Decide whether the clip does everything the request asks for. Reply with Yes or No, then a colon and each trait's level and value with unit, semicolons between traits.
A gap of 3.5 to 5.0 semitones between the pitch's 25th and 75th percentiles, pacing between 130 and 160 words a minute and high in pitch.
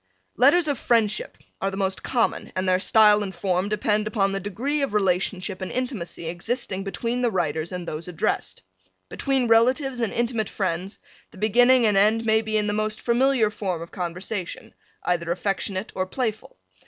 No: average, 3.8 semitones; average, 175 wpm; high, 210 Hz